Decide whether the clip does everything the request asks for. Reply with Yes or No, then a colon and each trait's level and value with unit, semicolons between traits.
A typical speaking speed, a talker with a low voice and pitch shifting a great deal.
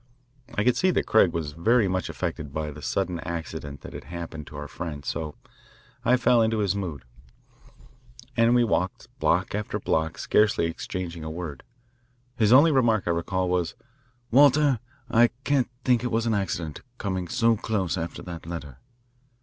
Yes: average, 170 wpm; very low, 95 Hz; wide, 5.9 semitones